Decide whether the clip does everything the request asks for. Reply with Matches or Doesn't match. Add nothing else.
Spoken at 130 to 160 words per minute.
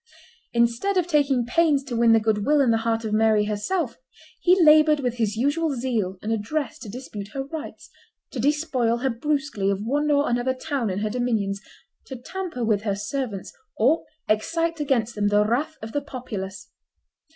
Doesn't match